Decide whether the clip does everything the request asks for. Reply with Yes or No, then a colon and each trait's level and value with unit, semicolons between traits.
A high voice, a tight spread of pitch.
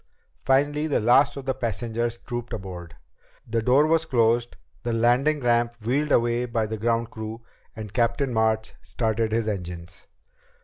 No: low, 115 Hz; narrow, 2.2 semitones